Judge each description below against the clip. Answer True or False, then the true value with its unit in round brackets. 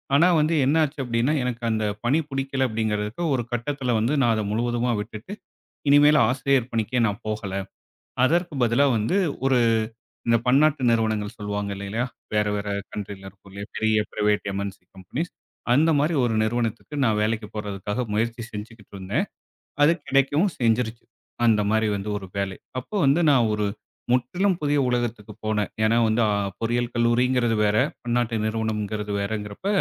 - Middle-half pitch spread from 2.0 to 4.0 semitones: True (3.7 semitones)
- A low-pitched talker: True (115 Hz)